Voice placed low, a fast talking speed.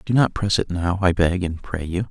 Yes: very low, 95 Hz; fast, 285 wpm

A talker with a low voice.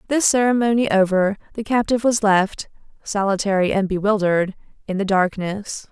No: high, 205 Hz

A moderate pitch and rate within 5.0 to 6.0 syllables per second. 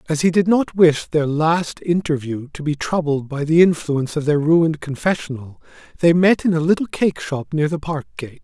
Yes: medium, 155 Hz; 5.3 syllables/s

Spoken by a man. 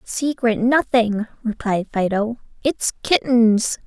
No: female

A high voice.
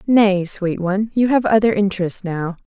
Yes: high, 200 Hz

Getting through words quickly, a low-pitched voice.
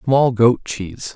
No: average, 155 wpm; low, 115 Hz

